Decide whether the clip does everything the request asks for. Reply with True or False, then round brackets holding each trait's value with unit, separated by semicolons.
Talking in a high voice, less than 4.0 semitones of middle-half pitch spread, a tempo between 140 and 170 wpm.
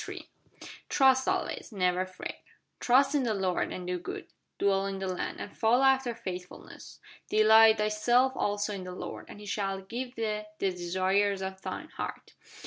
True (205 Hz; 3.6 semitones; 165 wpm)